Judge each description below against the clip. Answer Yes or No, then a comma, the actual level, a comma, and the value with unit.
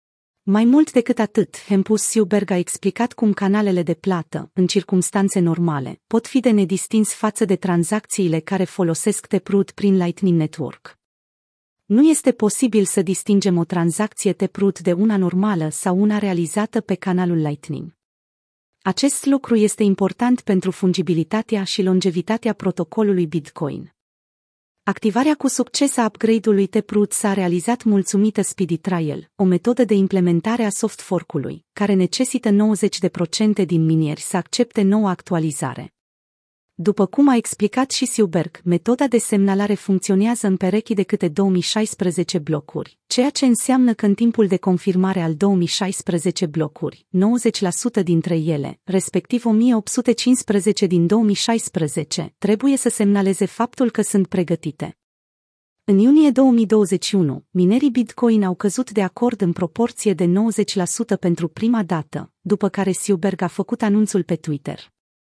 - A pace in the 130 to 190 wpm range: Yes, average, 135 wpm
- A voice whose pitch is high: Yes, high, 200 Hz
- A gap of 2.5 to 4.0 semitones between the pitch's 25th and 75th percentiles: Yes, average, 3.5 semitones